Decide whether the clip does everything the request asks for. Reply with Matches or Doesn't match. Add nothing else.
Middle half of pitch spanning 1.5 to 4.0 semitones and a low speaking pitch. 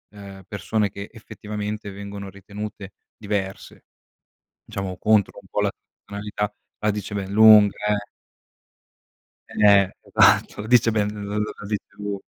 Doesn't match